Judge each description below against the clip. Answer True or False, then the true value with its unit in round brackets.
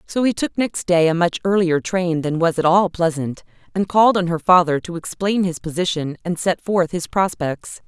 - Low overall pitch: False (175 Hz)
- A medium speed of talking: False (215 wpm)